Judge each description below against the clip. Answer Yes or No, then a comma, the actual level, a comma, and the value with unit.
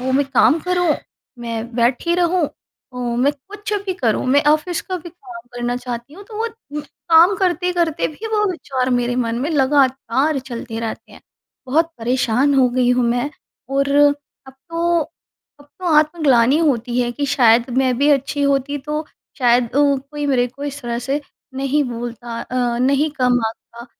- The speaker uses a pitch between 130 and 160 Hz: No, very high, 270 Hz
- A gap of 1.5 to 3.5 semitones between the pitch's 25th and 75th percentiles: No, average, 4.1 semitones